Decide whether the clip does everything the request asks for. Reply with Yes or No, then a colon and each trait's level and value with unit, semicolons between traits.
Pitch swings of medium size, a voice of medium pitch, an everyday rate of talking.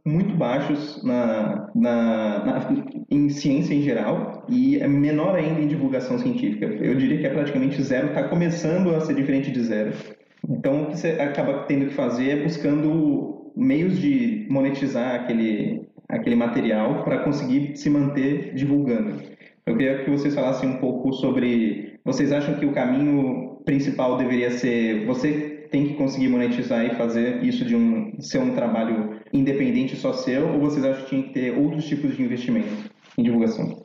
Yes: average, 4.3 semitones; medium, 145 Hz; average, 170 wpm